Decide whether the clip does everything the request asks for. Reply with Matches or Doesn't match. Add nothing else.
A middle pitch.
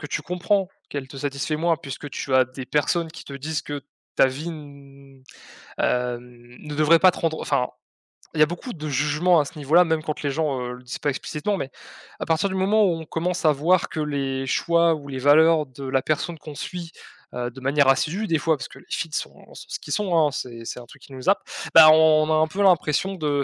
Matches